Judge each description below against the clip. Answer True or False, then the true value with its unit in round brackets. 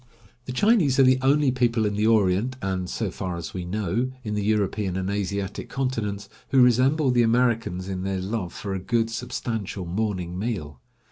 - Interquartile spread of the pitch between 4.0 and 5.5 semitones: True (4.6 semitones)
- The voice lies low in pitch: True (105 Hz)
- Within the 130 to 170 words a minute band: False (185 wpm)